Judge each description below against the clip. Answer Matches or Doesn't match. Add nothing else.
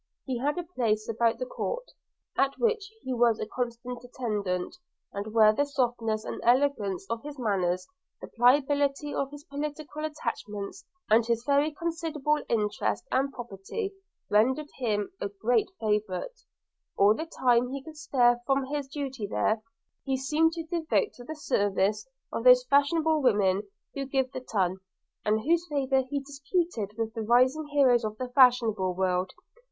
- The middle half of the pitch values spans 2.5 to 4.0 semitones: Doesn't match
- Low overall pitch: Doesn't match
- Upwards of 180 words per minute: Doesn't match